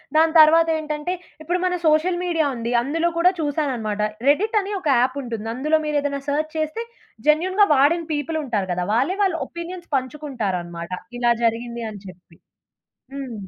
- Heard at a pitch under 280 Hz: No, very high, 295 Hz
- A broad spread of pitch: Yes, wide, 5.7 semitones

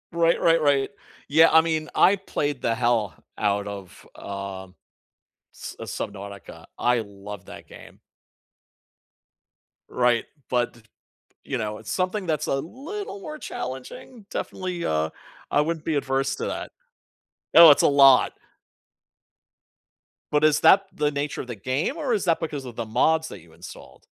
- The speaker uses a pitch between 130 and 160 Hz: Yes, medium, 140 Hz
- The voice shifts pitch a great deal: Yes, wide, 6.7 semitones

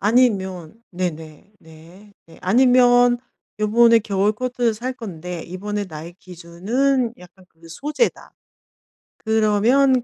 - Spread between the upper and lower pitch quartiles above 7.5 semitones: No, average, 5.3 semitones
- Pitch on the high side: Yes, high, 210 Hz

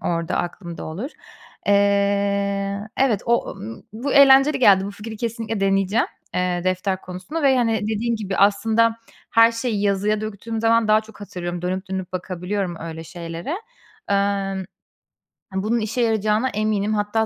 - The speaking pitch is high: Yes, high, 205 Hz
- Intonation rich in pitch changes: No, average, 2.9 semitones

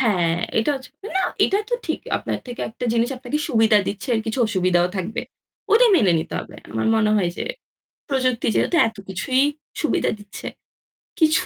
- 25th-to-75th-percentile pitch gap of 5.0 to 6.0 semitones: Yes, average, 5.3 semitones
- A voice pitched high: Yes, high, 225 Hz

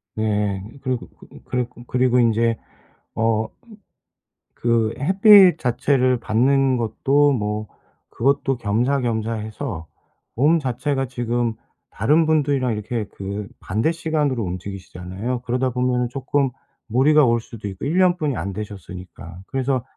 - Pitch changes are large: No, average, 4.1 semitones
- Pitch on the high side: No, low, 120 Hz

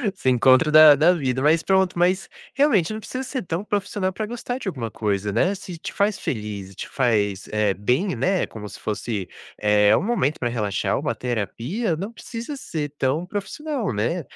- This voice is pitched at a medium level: Yes, medium, 155 Hz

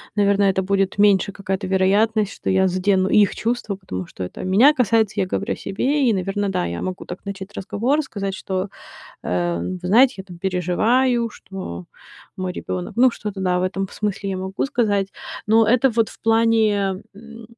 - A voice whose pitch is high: Yes, high, 200 Hz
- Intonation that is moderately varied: Yes, average, 3.0 semitones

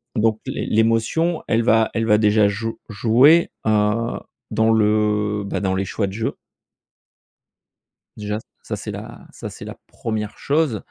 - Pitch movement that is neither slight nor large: No, narrow, 1.4 semitones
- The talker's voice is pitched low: Yes, low, 110 Hz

